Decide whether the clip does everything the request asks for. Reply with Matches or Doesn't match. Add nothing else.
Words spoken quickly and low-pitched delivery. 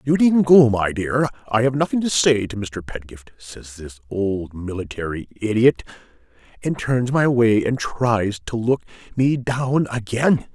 Doesn't match